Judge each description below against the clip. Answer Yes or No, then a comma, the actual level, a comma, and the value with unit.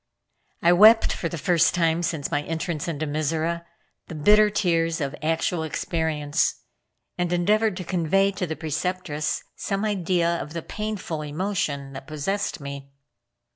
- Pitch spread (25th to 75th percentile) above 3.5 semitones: No, average, 3.2 semitones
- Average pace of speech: Yes, average, 145 wpm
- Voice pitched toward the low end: No, medium, 165 Hz